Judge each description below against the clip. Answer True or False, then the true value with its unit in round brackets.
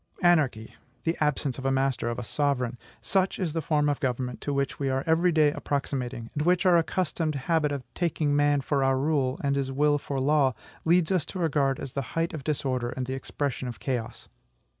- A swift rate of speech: True (210 wpm)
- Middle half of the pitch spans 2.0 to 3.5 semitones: True (3.0 semitones)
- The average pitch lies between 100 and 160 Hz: True (140 Hz)